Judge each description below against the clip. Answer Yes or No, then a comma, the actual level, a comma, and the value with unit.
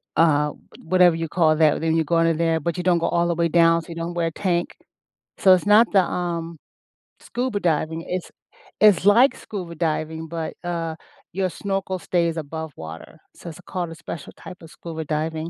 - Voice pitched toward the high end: No, medium, 170 Hz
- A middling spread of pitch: No, narrow, 1.8 semitones